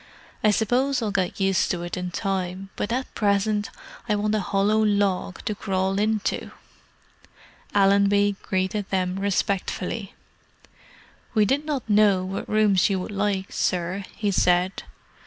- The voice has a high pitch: Yes, high, 200 Hz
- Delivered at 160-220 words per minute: No, average, 140 wpm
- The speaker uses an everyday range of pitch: No, narrow, 1.9 semitones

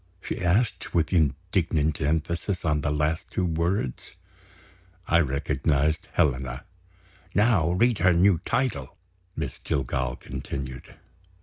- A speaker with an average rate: No, slow, 110 wpm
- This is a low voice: Yes, very low, 80 Hz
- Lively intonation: No, average, 4.0 semitones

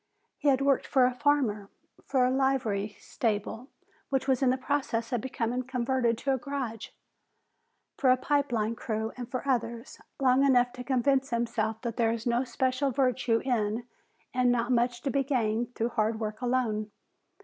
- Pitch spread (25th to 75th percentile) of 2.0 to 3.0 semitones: Yes, narrow, 2.5 semitones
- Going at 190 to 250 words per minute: No, average, 175 wpm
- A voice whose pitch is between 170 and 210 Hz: No, high, 245 Hz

